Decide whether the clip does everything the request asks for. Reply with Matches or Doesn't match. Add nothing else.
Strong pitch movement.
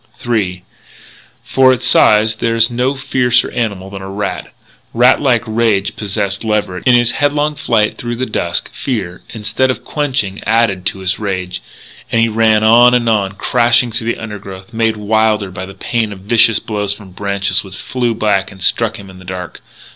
Doesn't match